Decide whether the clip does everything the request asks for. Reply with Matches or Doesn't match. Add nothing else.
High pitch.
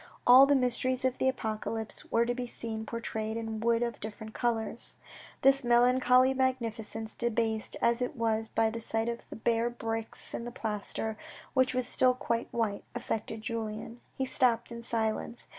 Matches